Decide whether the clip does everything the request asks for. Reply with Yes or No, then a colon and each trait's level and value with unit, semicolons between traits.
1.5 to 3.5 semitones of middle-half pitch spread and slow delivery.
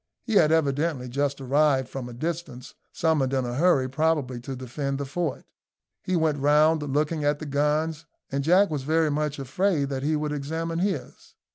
No: average, 3.0 semitones; average, 180 wpm